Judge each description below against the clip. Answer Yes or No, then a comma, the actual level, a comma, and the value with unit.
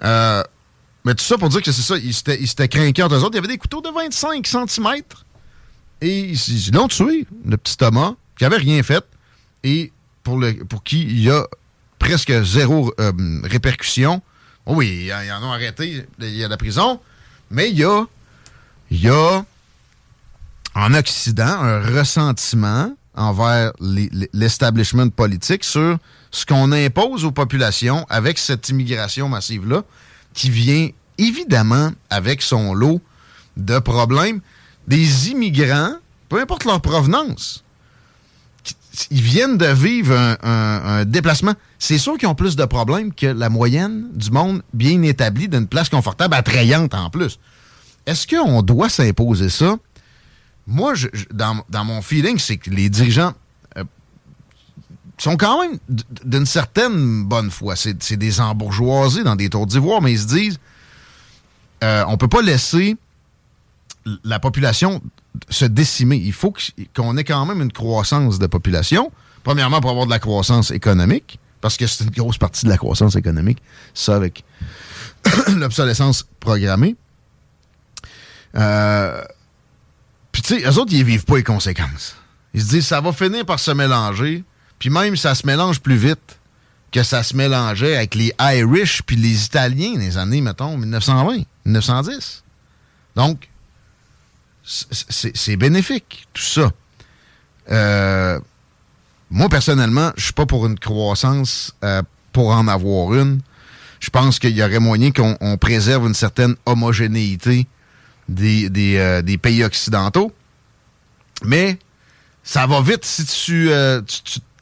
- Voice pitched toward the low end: Yes, low, 125 Hz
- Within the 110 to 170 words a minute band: Yes, average, 155 wpm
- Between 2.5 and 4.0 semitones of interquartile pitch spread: No, wide, 5.4 semitones